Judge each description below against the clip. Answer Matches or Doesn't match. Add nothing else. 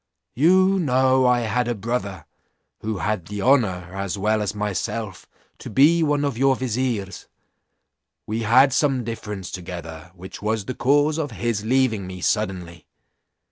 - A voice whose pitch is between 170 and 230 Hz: Doesn't match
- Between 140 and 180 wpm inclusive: Matches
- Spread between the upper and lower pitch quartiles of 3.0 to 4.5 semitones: Doesn't match